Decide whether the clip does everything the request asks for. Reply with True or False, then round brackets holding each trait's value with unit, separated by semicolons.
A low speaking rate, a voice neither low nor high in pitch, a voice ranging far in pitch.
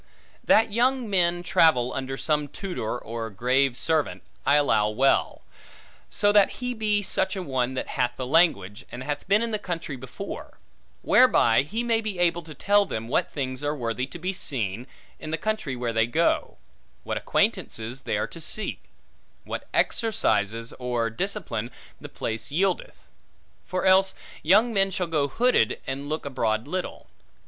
False (165 wpm; 150 Hz; 7.8 semitones)